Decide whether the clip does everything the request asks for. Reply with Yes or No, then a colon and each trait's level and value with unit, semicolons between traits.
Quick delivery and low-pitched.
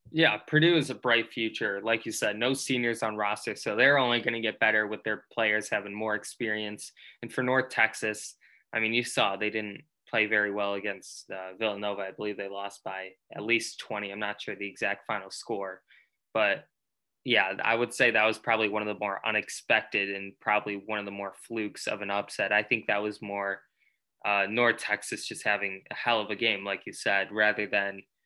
Yes: fast, 210 wpm; low, 105 Hz